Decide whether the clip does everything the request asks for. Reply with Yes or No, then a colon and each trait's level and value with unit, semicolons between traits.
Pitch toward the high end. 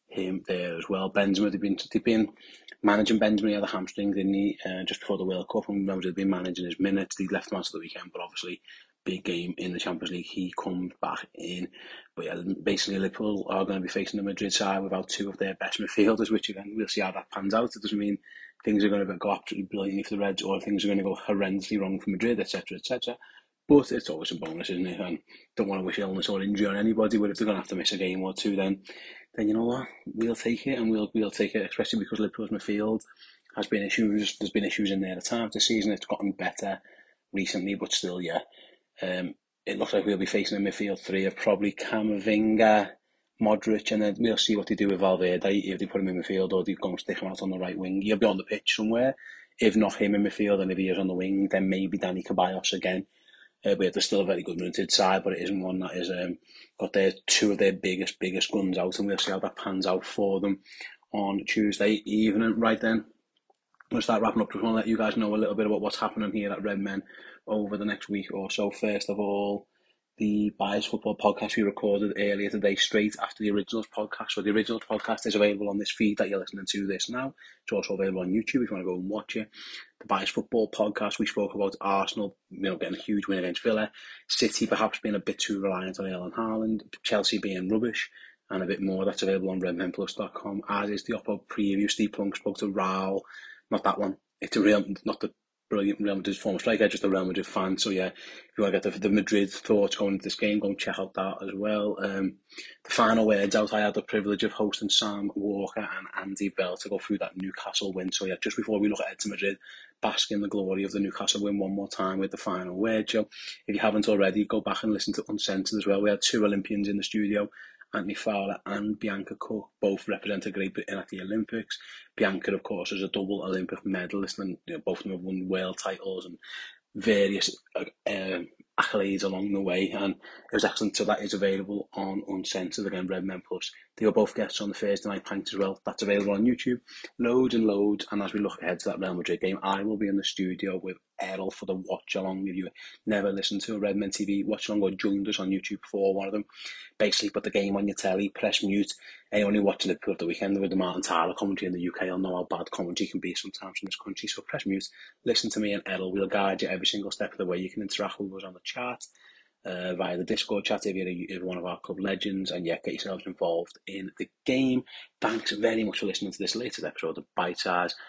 No: low, 100 Hz